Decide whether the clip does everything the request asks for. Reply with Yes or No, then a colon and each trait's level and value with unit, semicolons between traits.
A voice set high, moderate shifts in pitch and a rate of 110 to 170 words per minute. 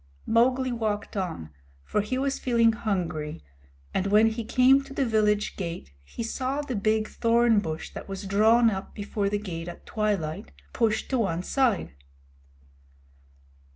Yes: high, 215 Hz; average, 3.5 semitones; average, 155 wpm